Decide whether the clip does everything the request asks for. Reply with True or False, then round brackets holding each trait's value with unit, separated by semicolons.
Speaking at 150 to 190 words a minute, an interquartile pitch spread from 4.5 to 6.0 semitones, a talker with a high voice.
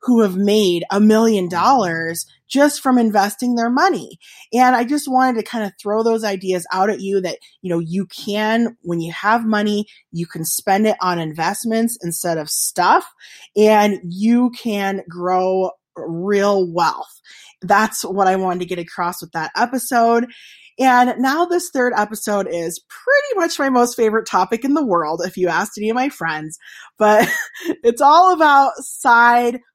True (170 wpm; 5.0 semitones; 210 Hz)